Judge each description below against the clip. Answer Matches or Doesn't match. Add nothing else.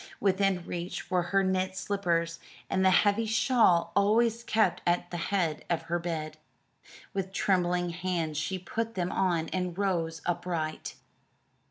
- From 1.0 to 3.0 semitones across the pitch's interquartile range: Matches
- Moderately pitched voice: Matches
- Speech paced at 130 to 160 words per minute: Matches